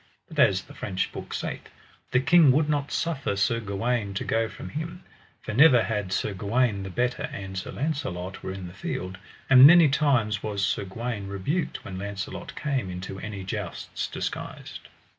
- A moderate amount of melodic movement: No, wide, 5.8 semitones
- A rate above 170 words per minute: Yes, average, 180 wpm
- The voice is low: Yes, low, 105 Hz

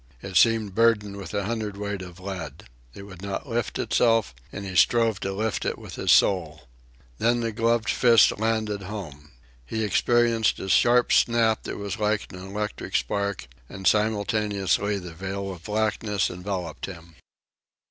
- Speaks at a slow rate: No, average, 155 wpm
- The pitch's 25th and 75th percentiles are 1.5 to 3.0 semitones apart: Yes, average, 2.7 semitones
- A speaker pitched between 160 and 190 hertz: No, low, 100 Hz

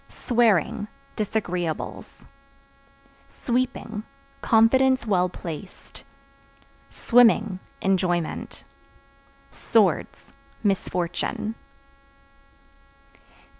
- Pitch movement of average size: Yes, average, 4.3 semitones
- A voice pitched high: Yes, high, 210 Hz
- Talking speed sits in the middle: No, slow, 45 wpm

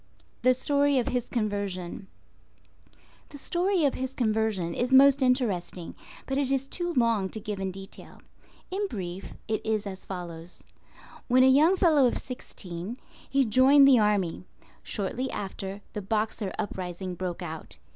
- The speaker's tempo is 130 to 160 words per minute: Yes, average, 145 wpm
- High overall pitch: Yes, high, 220 Hz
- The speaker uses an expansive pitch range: Yes, wide, 5.7 semitones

